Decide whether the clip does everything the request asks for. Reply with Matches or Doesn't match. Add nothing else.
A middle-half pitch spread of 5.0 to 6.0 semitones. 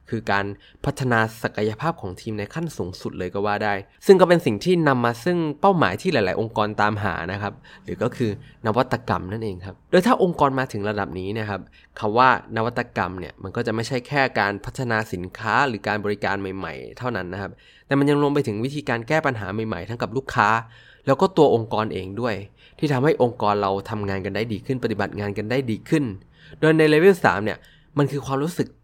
Matches